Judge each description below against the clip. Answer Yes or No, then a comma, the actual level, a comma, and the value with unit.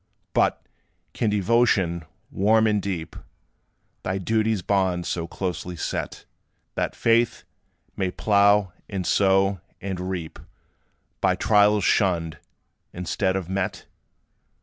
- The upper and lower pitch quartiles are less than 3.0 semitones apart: Yes, narrow, 2.5 semitones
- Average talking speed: No, slow, 105 wpm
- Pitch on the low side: Yes, very low, 95 Hz